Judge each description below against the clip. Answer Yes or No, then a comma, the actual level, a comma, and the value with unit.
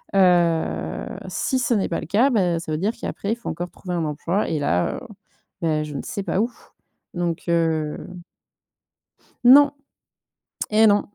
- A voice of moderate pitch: Yes, medium, 175 Hz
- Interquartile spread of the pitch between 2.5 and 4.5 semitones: No, average, 5.0 semitones